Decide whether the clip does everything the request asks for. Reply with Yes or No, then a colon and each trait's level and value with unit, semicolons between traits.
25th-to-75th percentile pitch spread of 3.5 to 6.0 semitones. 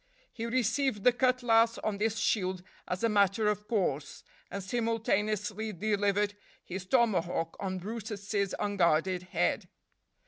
No: average, 3.1 semitones